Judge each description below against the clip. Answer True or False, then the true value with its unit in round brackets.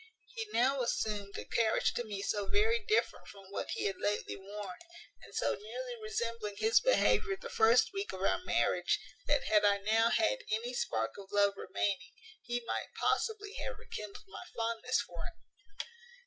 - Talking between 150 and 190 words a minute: True (175 wpm)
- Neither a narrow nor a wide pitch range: False (8.6 semitones)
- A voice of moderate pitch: False (225 Hz)